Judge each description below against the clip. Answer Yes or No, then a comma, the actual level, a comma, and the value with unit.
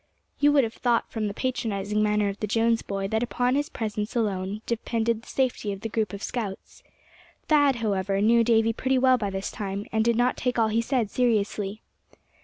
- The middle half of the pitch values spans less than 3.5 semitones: Yes, average, 2.8 semitones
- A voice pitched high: Yes, high, 225 Hz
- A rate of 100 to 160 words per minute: No, fast, 205 wpm